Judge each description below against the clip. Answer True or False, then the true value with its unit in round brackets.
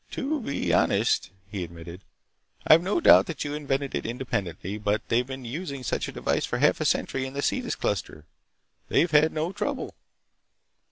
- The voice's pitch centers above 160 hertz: False (135 Hz)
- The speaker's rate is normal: True (175 wpm)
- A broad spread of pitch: True (7.1 semitones)